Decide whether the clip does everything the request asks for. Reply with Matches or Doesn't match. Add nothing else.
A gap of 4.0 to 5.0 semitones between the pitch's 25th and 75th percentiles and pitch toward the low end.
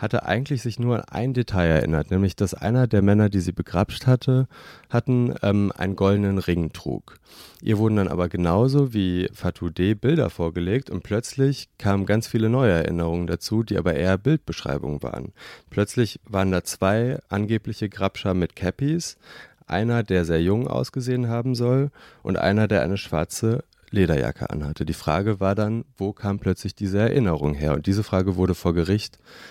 Matches